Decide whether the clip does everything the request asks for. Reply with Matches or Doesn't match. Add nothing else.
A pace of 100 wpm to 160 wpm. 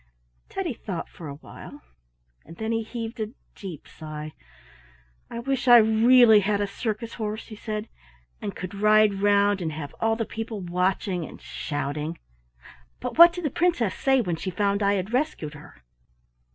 Doesn't match